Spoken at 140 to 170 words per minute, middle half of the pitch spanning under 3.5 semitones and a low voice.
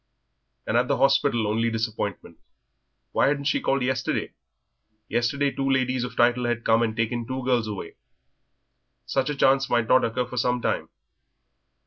Yes: average, 160 wpm; narrow, 2.5 semitones; low, 125 Hz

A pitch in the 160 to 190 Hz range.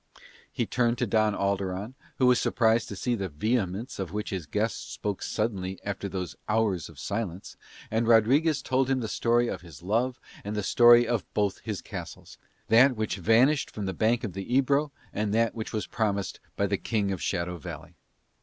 No: low, 110 Hz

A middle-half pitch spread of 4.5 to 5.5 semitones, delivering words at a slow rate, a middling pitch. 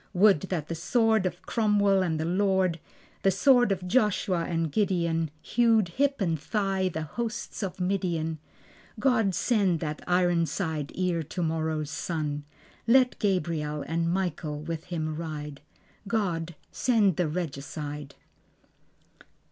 No: average, 3.8 semitones; slow, 125 wpm; medium, 175 Hz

